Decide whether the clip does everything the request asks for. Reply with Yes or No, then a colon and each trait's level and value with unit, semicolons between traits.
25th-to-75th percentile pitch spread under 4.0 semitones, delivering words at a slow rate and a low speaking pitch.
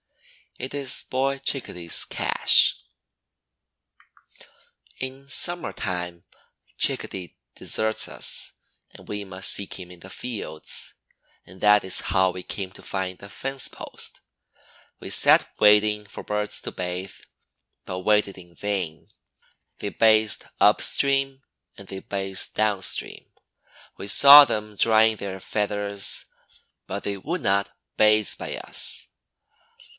Yes: average, 2.7 semitones; slow, 125 wpm; low, 105 Hz